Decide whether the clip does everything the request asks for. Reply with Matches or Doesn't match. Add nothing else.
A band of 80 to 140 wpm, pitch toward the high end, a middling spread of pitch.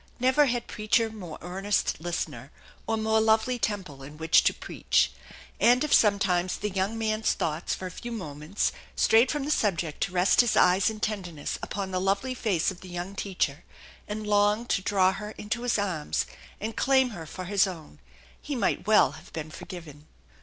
Doesn't match